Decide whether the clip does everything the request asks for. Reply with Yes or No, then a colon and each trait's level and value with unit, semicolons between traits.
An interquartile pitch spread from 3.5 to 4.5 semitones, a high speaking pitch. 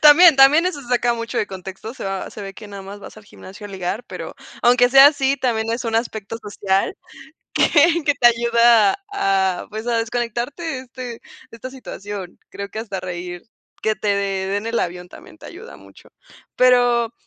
Yes: average, 3.9 semitones; high, 230 Hz